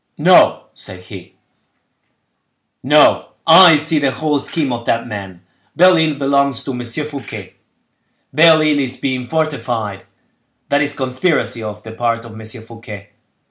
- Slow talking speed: No, average, 145 wpm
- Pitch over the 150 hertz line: No, low, 130 Hz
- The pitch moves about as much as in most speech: Yes, average, 4.7 semitones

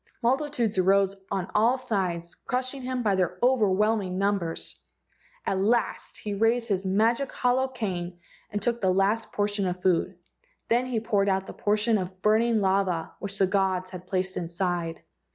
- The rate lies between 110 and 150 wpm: No, average, 160 wpm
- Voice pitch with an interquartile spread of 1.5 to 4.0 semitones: Yes, average, 3.6 semitones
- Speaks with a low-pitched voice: No, high, 200 Hz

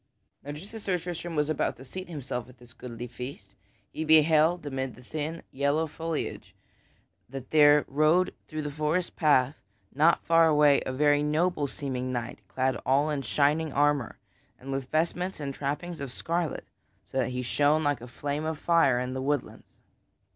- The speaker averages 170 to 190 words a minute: Yes, average, 175 wpm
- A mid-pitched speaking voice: Yes, medium, 145 Hz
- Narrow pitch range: No, average, 3.1 semitones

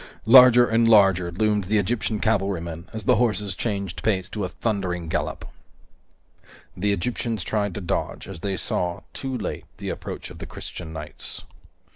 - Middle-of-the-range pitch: No, low, 100 Hz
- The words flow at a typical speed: Yes, average, 160 wpm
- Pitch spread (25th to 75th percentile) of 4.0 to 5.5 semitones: No, average, 3.6 semitones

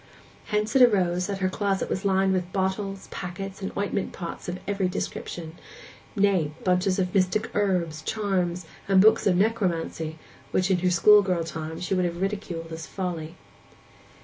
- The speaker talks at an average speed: Yes, average, 155 wpm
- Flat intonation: Yes, narrow, 2.2 semitones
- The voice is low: No, medium, 185 Hz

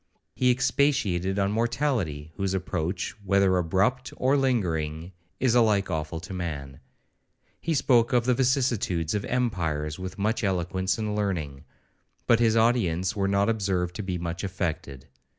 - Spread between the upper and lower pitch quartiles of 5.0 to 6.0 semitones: Yes, average, 5.3 semitones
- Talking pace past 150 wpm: No, average, 140 wpm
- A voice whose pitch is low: Yes, very low, 95 Hz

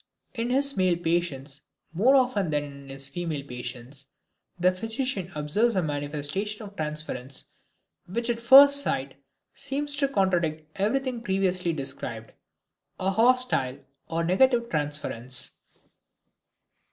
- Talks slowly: Yes, slow, 115 wpm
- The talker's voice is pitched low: No, medium, 180 Hz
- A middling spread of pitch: No, wide, 8.3 semitones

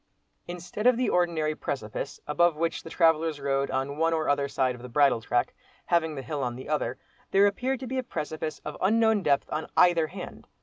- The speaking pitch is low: No, medium, 155 Hz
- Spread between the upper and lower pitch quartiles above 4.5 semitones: No, average, 4.0 semitones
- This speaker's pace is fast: Yes, fast, 210 wpm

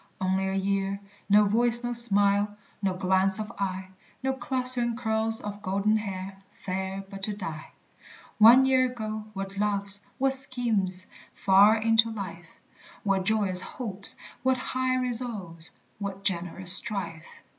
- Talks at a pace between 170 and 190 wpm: No, slow, 135 wpm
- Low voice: No, high, 205 Hz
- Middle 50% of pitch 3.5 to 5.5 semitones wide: No, average, 3.1 semitones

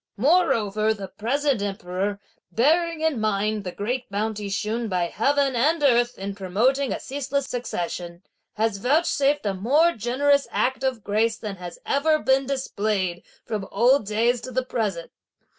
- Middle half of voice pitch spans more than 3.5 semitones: Yes, average, 5.2 semitones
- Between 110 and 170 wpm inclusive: Yes, average, 150 wpm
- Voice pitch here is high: Yes, high, 230 Hz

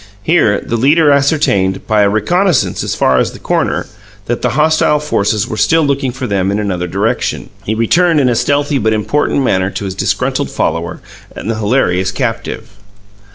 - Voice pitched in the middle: No, low, 115 Hz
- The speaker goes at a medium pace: Yes, average, 180 wpm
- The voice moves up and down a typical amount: No, wide, 6.3 semitones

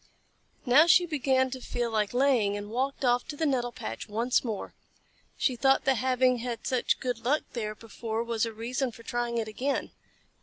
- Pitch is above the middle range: Yes, high, 245 Hz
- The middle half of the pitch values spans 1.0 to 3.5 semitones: Yes, narrow, 2.6 semitones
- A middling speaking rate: Yes, average, 190 wpm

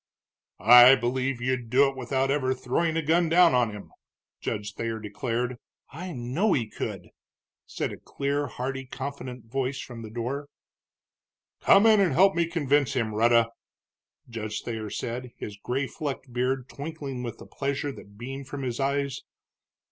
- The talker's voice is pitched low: Yes, low, 130 Hz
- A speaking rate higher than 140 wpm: Yes, average, 160 wpm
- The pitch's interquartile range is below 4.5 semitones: Yes, average, 3.0 semitones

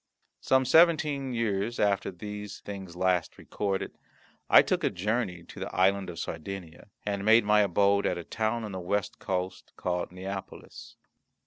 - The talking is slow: No, average, 155 wpm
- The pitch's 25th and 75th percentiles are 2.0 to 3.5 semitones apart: Yes, average, 2.9 semitones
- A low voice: Yes, low, 100 Hz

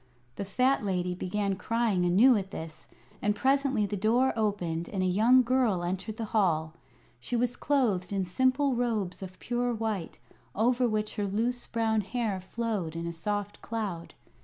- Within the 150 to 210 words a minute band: Yes, average, 165 wpm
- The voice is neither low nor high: No, high, 210 Hz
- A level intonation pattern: No, average, 4.4 semitones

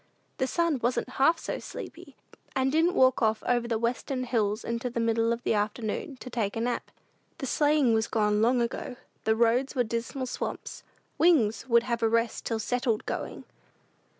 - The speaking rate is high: No, average, 180 wpm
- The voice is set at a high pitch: Yes, high, 235 Hz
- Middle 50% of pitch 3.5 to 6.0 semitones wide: No, narrow, 2.5 semitones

